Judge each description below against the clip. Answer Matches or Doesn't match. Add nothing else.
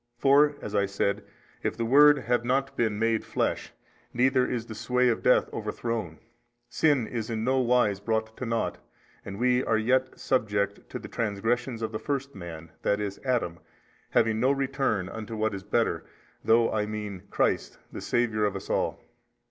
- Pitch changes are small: Doesn't match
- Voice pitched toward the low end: Matches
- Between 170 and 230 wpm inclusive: Matches